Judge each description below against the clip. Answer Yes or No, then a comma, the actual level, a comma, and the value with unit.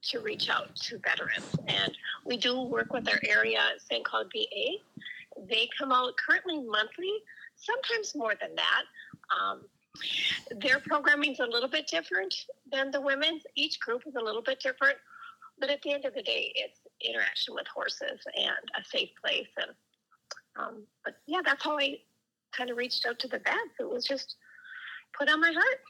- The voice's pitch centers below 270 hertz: No, very high, 300 Hz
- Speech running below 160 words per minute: No, average, 180 wpm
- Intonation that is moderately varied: No, wide, 9.0 semitones